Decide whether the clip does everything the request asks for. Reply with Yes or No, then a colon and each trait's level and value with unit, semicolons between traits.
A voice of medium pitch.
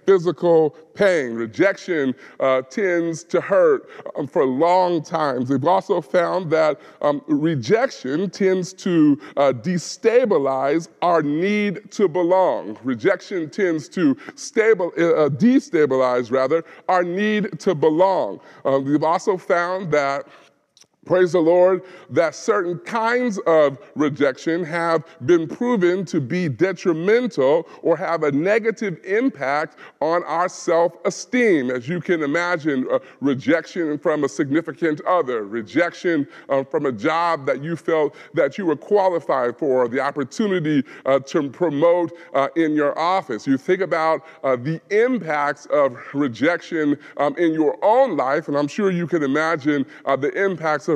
Yes: medium, 170 Hz